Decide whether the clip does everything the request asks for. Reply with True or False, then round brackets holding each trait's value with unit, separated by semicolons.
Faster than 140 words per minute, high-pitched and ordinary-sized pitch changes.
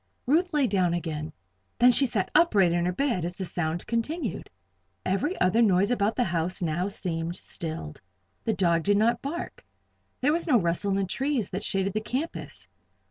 False (185 wpm; 195 Hz; 6.1 semitones)